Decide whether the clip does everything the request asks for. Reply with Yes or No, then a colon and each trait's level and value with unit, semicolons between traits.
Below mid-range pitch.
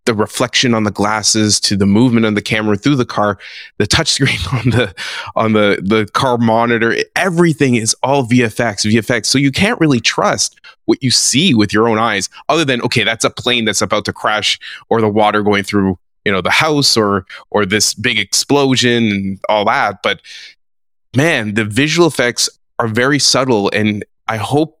Yes: low, 115 Hz